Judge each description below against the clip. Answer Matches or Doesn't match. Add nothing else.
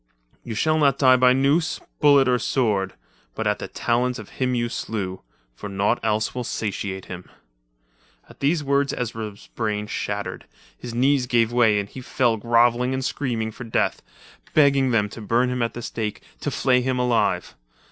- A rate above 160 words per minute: Matches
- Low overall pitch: Matches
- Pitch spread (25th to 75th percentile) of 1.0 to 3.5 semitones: Matches